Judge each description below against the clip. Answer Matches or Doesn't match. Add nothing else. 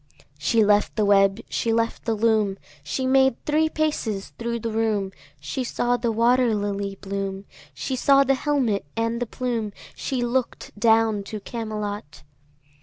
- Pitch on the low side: Doesn't match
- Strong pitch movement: Doesn't match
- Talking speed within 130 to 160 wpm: Matches